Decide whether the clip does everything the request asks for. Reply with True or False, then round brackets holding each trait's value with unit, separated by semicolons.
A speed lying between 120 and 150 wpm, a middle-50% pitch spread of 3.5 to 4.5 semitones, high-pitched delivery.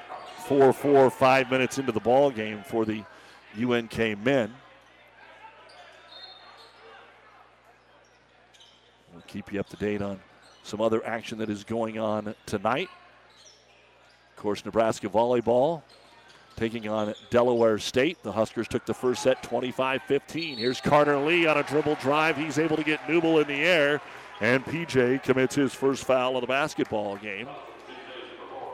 False (140 wpm; 4.1 semitones; 125 Hz)